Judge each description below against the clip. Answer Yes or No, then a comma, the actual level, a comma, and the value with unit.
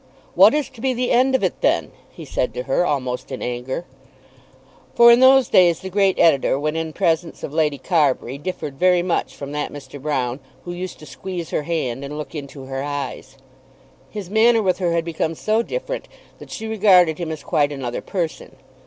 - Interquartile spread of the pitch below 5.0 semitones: No, average, 5.3 semitones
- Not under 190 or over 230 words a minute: Yes, average, 200 wpm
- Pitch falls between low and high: Yes, medium, 165 Hz